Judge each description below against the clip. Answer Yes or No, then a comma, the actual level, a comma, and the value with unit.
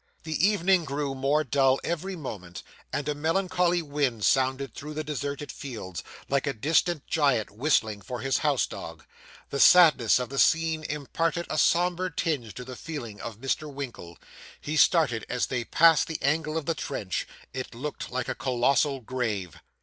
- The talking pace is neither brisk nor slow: Yes, average, 170 wpm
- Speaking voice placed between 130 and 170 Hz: Yes, medium, 140 Hz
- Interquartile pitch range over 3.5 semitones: Yes, average, 4.2 semitones